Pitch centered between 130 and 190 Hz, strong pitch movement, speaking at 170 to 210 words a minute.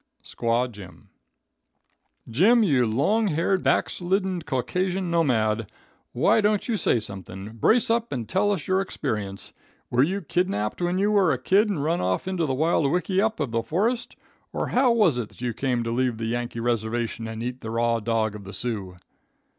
Yes: low, 135 Hz; wide, 8.7 semitones; average, 180 wpm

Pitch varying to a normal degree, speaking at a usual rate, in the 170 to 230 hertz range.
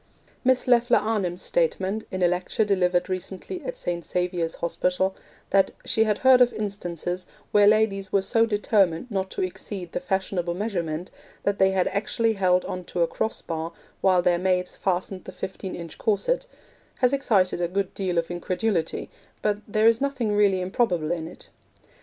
Yes: average, 3.3 semitones; average, 170 wpm; high, 190 Hz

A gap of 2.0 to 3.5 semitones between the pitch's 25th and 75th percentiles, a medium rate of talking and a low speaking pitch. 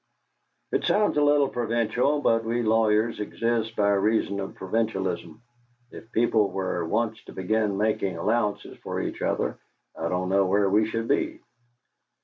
Yes: average, 2.8 semitones; average, 150 wpm; low, 110 Hz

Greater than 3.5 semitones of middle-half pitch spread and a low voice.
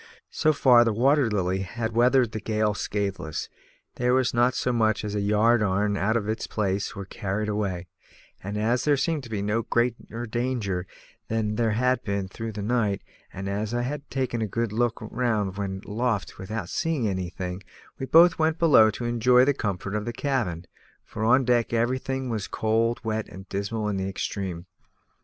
No: average, 3.2 semitones; low, 110 Hz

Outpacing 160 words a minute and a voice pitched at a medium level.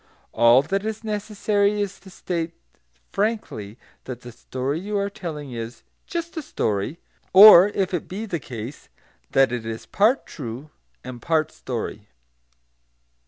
No: average, 145 wpm; medium, 165 Hz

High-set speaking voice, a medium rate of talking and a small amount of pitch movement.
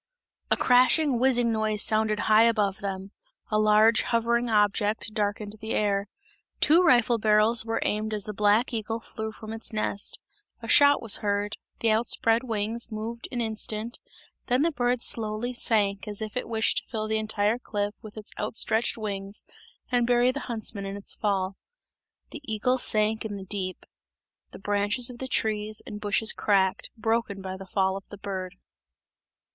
Yes: high, 215 Hz; average, 175 wpm; narrow, 2.1 semitones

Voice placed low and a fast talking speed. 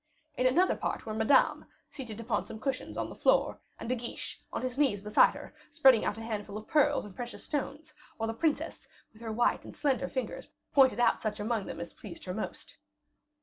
No: high, 235 Hz; fast, 215 wpm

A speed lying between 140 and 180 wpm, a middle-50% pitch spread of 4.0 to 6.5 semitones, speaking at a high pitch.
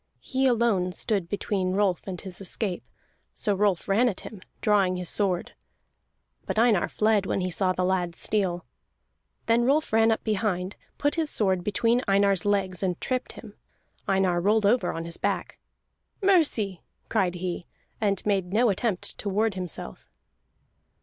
No: average, 155 wpm; average, 3.2 semitones; high, 200 Hz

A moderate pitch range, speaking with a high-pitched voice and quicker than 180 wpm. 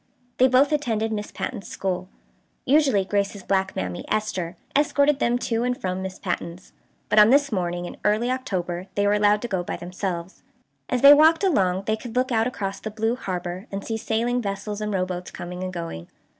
Yes: average, 4.8 semitones; high, 205 Hz; average, 195 wpm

